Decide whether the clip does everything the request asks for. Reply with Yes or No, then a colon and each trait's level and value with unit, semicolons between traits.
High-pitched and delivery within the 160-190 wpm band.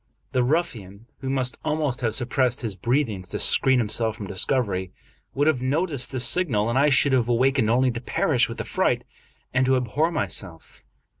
No: low, 125 Hz; average, 175 wpm